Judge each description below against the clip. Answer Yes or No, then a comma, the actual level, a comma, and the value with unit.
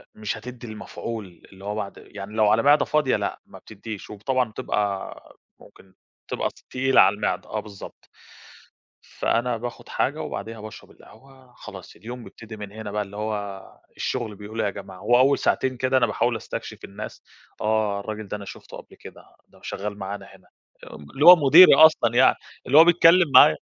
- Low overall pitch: Yes, low, 110 Hz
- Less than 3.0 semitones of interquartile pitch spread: No, average, 3.7 semitones